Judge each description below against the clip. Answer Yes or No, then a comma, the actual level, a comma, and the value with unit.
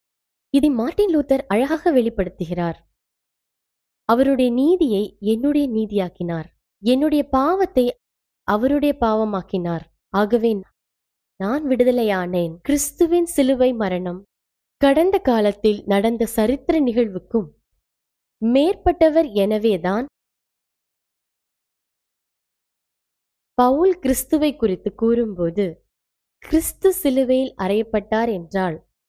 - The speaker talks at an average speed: No, slow, 70 wpm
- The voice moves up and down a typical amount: No, wide, 6.2 semitones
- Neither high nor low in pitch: No, high, 230 Hz